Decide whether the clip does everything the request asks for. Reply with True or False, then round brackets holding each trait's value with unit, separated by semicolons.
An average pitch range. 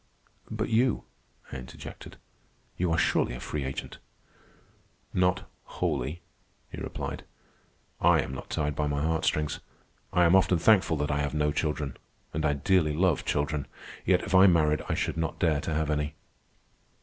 True (3.2 semitones)